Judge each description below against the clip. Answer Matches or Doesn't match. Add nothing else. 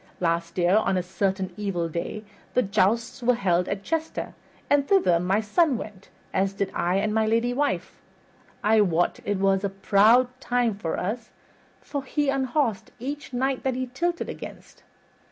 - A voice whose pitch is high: Matches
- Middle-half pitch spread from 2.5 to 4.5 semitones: Doesn't match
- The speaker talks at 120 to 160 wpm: Doesn't match